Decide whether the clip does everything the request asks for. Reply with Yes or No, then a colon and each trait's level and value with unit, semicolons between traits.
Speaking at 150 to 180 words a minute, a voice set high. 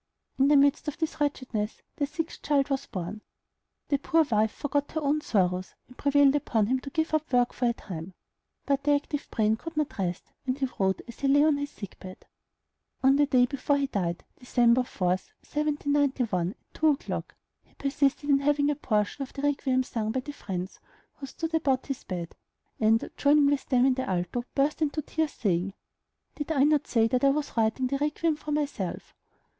No: average, 200 wpm; very high, 275 Hz